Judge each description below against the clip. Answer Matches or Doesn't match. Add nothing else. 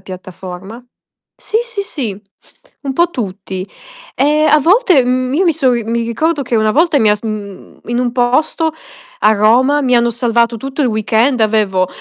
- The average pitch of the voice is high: Matches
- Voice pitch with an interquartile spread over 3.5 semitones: Matches